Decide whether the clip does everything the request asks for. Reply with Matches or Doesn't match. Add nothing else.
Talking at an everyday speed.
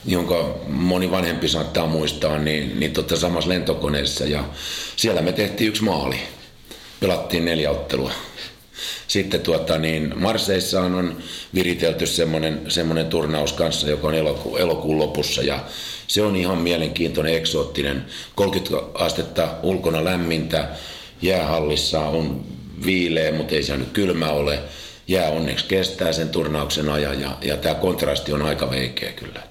Matches